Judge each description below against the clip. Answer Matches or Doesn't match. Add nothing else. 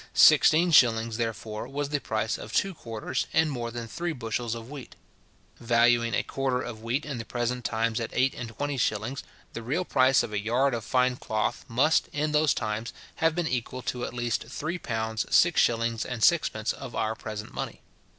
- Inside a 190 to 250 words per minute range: Matches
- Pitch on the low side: Matches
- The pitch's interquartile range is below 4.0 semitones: Matches